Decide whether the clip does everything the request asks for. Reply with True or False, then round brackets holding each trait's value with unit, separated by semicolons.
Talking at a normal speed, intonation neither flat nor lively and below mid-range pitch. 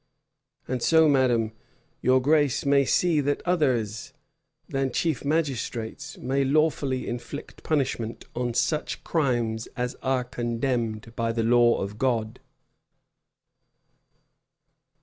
False (110 wpm; 3.3 semitones; 130 Hz)